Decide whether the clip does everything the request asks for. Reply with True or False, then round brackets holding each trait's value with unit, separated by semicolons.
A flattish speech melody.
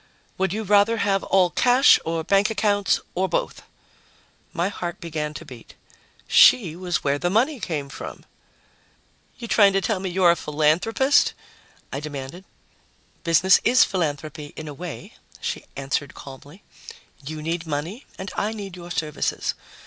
False (4.8 semitones)